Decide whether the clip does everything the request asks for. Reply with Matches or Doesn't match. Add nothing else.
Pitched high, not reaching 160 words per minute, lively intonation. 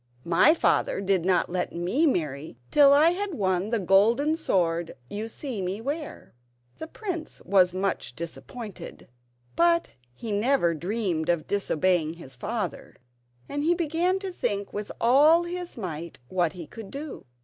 Matches